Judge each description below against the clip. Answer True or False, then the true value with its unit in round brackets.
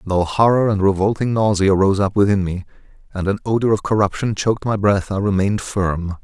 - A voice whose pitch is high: False (100 Hz)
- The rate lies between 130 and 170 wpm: False (195 wpm)